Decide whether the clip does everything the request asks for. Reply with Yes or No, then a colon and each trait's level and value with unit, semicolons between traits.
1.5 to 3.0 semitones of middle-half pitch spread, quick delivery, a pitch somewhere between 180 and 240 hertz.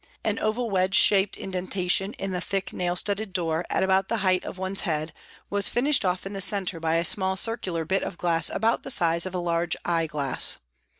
Yes: narrow, 2.4 semitones; fast, 215 wpm; medium, 185 Hz